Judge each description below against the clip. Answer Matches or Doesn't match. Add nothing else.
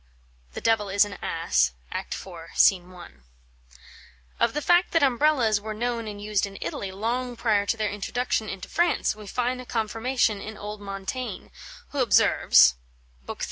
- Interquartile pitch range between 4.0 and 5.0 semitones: Doesn't match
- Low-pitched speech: Doesn't match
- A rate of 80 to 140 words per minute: Doesn't match